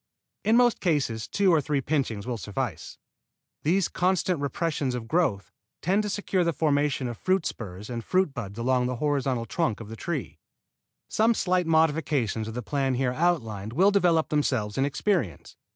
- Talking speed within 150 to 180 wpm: Yes, average, 170 wpm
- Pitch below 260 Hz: Yes, medium, 140 Hz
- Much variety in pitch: Yes, wide, 6.8 semitones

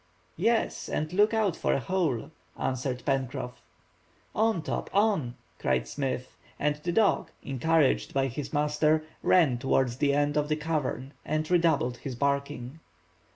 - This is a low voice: No, medium, 145 Hz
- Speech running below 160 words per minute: Yes, average, 145 wpm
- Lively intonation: No, average, 3.8 semitones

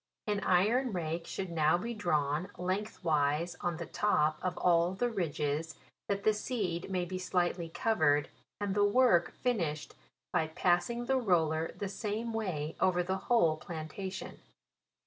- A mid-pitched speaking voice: Yes, medium, 180 Hz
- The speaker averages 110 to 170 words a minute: Yes, average, 150 wpm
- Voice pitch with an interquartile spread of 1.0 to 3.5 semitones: No, average, 4.2 semitones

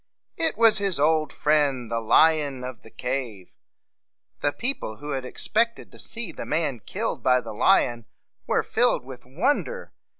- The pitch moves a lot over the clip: Yes, wide, 7.8 semitones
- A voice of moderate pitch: Yes, medium, 145 Hz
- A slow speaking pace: No, average, 170 wpm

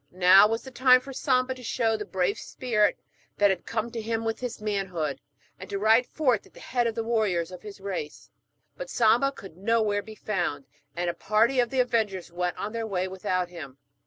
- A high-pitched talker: Yes, high, 215 Hz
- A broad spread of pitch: No, average, 4.0 semitones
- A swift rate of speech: Yes, fast, 215 wpm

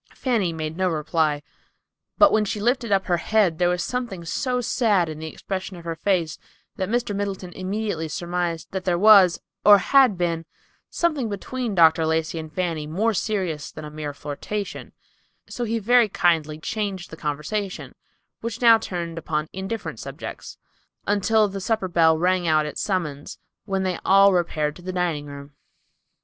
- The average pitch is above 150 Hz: Yes, medium, 185 Hz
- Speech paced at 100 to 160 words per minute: No, average, 170 wpm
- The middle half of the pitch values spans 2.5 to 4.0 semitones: No, average, 4.5 semitones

